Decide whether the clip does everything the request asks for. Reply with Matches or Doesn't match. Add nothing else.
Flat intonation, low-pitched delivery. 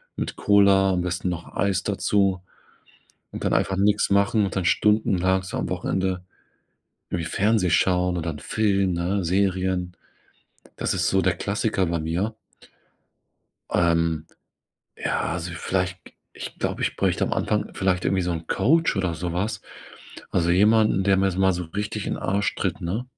Matches